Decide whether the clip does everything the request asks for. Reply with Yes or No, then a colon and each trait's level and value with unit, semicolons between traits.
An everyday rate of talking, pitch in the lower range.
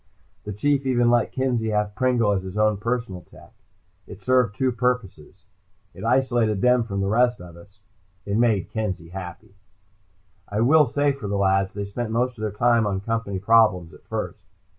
Yes: average, 185 wpm; low, 110 Hz